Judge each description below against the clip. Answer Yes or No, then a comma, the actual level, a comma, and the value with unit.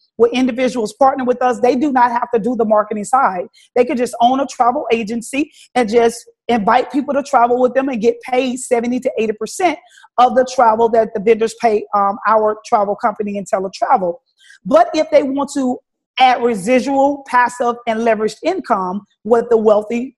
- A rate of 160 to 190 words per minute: Yes, average, 185 wpm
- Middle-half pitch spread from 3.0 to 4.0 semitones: No, narrow, 2.4 semitones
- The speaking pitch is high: Yes, high, 240 Hz